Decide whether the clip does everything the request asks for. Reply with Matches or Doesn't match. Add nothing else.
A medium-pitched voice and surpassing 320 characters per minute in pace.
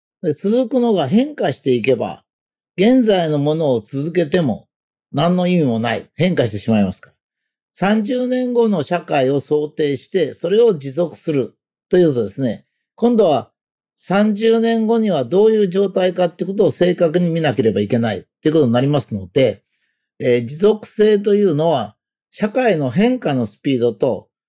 Doesn't match